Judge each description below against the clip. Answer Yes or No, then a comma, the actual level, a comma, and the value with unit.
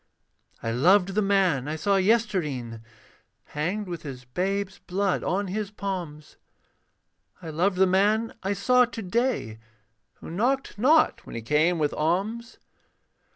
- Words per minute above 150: No, average, 140 wpm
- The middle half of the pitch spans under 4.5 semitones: No, average, 5.1 semitones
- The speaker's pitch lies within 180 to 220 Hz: Yes, high, 190 Hz